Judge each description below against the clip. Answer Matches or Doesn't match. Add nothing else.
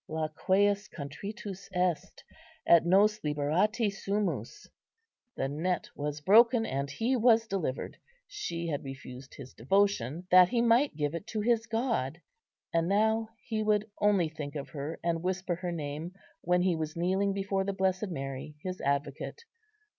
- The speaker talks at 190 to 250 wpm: Doesn't match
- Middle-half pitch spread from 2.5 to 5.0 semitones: Doesn't match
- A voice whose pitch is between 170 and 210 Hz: Matches